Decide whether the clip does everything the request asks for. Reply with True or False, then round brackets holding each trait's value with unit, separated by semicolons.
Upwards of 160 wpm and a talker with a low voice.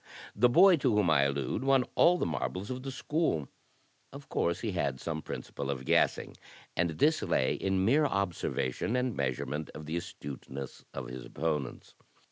True (170 wpm; 85 Hz)